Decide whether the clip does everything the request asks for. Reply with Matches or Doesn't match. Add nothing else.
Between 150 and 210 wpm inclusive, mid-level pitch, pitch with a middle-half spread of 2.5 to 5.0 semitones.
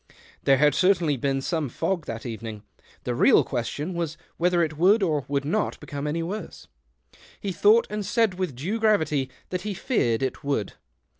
Doesn't match